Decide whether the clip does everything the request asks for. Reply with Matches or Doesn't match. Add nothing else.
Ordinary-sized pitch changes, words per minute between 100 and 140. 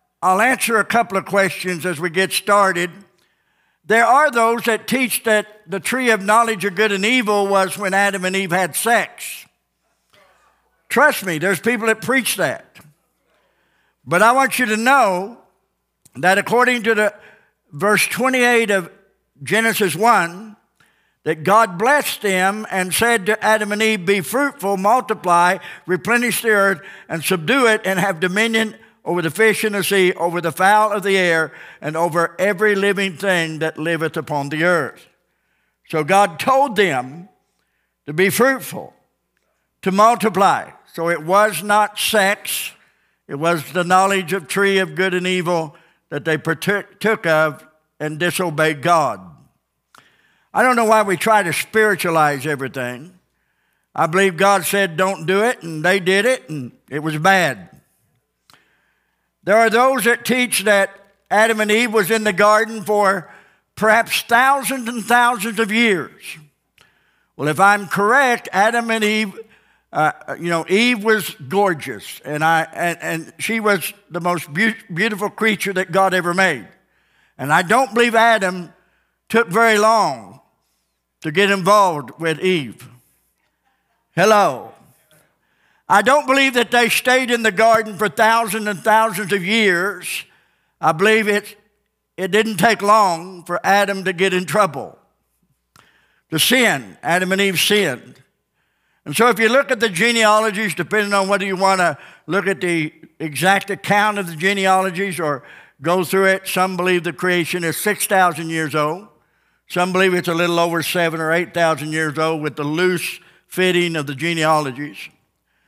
Doesn't match